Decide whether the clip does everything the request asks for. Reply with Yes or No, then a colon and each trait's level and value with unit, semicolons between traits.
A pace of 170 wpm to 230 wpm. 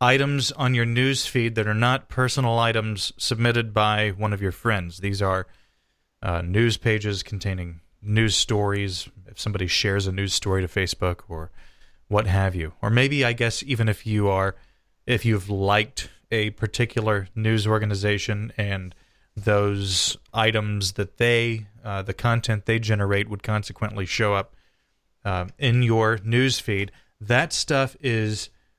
No: average, 150 wpm